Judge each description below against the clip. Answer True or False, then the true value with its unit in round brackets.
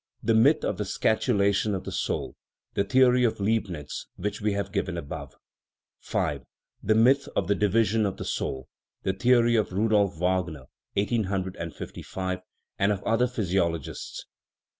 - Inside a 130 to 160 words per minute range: True (145 wpm)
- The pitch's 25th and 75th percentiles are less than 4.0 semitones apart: True (3.3 semitones)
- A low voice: True (100 Hz)